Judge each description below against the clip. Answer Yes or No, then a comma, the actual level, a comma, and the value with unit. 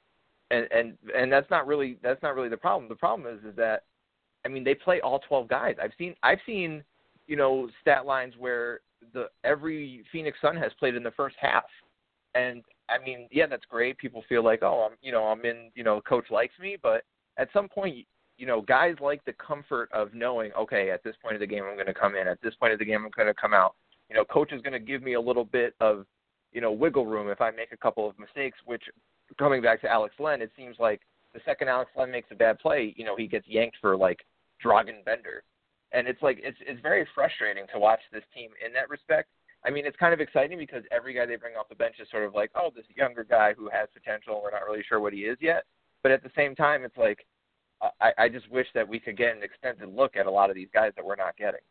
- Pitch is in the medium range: No, low, 120 Hz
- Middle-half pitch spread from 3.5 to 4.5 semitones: Yes, average, 3.9 semitones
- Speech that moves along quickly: Yes, fast, 255 wpm